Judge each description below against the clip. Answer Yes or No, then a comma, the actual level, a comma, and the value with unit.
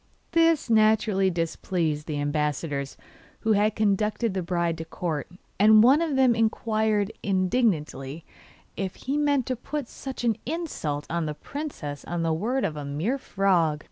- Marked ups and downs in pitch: Yes, wide, 6.7 semitones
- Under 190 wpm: Yes, average, 155 wpm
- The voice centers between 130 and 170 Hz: No, high, 195 Hz